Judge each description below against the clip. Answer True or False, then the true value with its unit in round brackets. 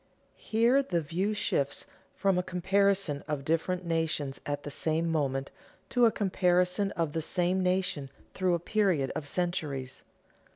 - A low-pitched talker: False (175 Hz)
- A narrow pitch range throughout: False (4.3 semitones)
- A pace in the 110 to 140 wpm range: False (155 wpm)